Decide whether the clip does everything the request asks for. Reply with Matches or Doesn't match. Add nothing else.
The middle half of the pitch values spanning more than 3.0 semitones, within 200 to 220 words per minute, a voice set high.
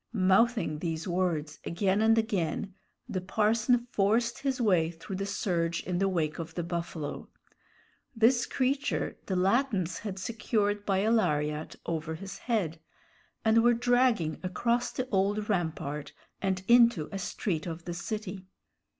Doesn't match